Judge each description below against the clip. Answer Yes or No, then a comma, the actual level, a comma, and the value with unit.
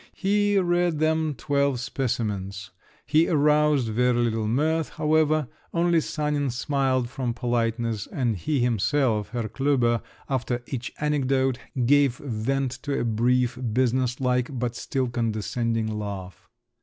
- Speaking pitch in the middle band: No, low, 125 Hz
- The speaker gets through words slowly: Yes, slow, 125 wpm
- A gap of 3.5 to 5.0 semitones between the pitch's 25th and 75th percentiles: Yes, average, 3.8 semitones